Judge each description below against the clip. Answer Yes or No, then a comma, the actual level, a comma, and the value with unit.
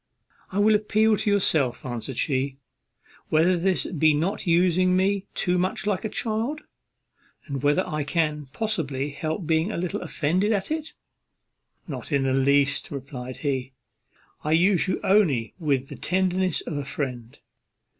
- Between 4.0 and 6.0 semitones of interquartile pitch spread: Yes, average, 5.3 semitones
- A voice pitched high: No, medium, 165 Hz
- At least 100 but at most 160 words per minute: Yes, average, 155 wpm